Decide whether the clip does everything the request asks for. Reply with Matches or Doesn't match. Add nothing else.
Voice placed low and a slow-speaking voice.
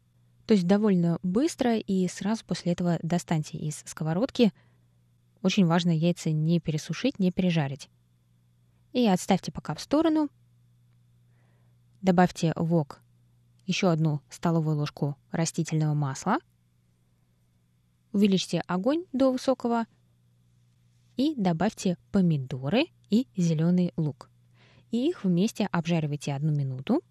Doesn't match